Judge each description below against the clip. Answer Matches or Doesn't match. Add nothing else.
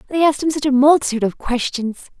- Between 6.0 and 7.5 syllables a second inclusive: Matches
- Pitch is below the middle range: Doesn't match